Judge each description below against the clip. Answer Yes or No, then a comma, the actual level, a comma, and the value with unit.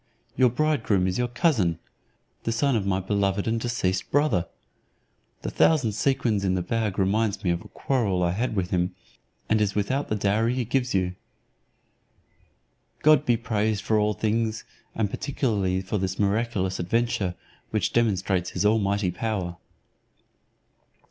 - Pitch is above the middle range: No, low, 105 Hz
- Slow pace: No, average, 150 wpm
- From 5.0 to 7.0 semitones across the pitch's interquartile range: No, average, 3.8 semitones